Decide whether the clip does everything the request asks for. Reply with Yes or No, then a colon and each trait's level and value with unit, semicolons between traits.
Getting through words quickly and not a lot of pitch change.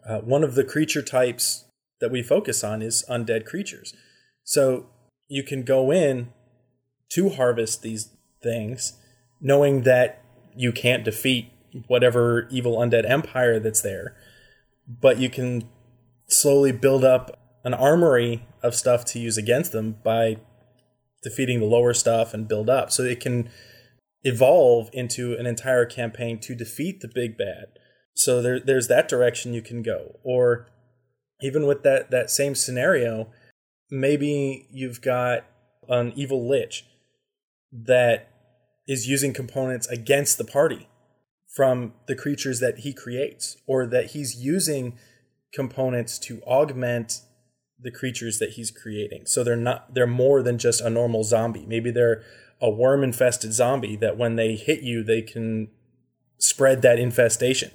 No: average, 145 wpm; narrow, 2.0 semitones